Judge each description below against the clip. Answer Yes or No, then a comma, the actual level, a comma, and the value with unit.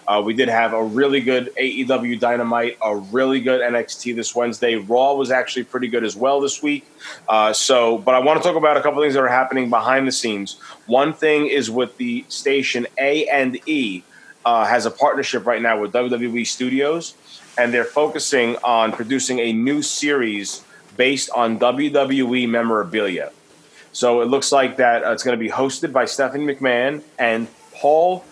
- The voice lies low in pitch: Yes, low, 130 Hz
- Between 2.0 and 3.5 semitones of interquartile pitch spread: Yes, average, 2.9 semitones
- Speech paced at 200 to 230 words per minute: No, average, 185 wpm